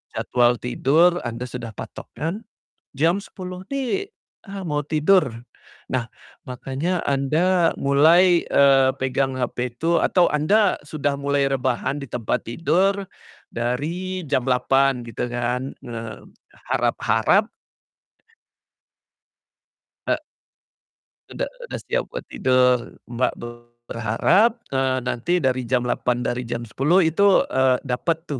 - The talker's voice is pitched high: No, low, 135 Hz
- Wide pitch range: Yes, wide, 5.9 semitones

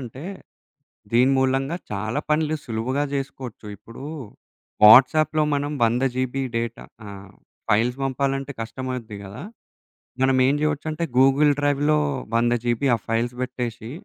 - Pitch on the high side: No, low, 130 Hz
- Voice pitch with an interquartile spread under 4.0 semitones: Yes, average, 3.3 semitones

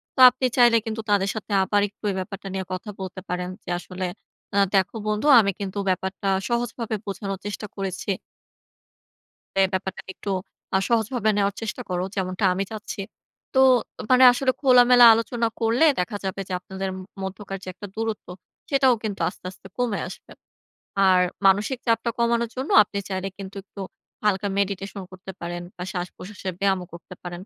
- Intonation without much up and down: No, average, 3.1 semitones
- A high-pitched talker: Yes, high, 200 Hz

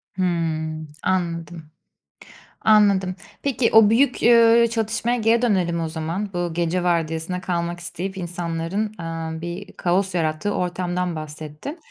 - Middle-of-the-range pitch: Yes, medium, 175 Hz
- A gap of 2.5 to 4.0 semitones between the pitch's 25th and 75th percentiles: Yes, average, 3.7 semitones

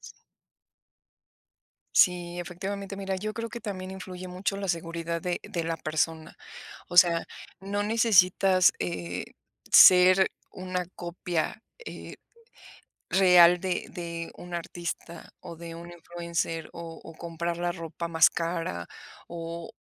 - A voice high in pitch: No, medium, 175 Hz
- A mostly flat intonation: Yes, narrow, 1.9 semitones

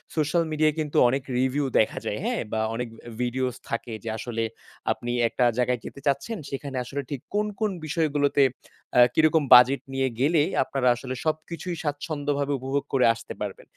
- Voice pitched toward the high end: No, medium, 140 Hz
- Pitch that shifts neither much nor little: Yes, average, 3.5 semitones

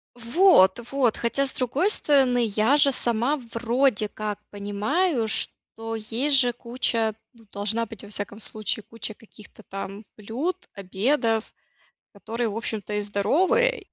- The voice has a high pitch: Yes, high, 230 Hz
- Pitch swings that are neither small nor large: Yes, average, 4.1 semitones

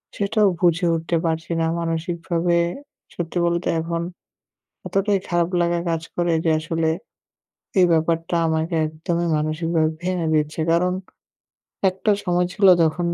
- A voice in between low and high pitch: Yes, medium, 170 Hz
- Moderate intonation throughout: No, narrow, 1.5 semitones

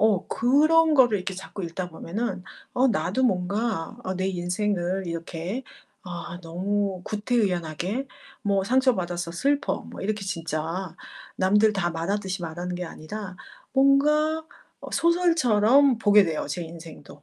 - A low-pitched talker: No, high, 195 Hz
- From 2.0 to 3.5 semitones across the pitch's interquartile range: No, wide, 5.5 semitones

